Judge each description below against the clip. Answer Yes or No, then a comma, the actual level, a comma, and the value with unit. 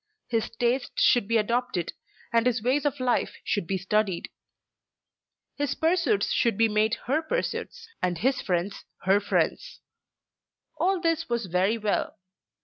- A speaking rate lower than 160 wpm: Yes, average, 140 wpm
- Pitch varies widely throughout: Yes, wide, 5.8 semitones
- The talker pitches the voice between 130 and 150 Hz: No, high, 230 Hz